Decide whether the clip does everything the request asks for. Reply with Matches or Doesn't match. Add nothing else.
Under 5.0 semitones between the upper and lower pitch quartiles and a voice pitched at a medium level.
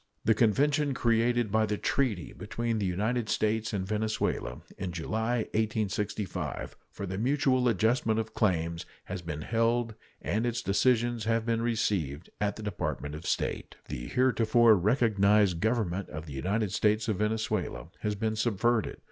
Doesn't match